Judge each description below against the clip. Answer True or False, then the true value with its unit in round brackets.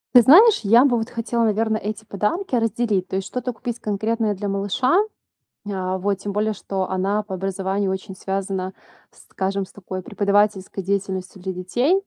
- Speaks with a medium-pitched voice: False (200 Hz)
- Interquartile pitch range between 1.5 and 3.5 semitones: True (2.9 semitones)